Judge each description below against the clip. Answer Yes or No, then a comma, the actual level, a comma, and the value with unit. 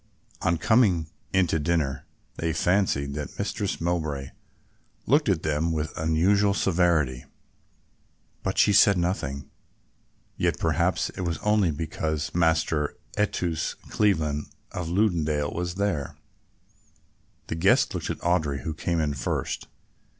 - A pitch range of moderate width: Yes, average, 3.2 semitones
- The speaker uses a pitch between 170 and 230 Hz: No, very low, 80 Hz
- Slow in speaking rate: Yes, slow, 125 wpm